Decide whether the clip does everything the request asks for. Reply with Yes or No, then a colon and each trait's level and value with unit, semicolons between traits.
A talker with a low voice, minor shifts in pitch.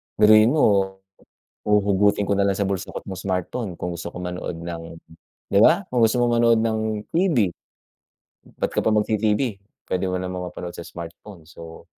No: low, 100 Hz; average, 3.5 semitones